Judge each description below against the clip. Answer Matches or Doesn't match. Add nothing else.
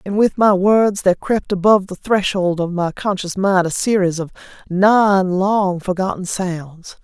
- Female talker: Matches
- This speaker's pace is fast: Doesn't match